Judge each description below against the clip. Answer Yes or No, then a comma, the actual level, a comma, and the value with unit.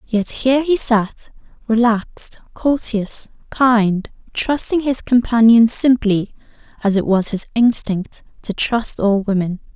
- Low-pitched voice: No, high, 225 Hz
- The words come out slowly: Yes, slow, 125 wpm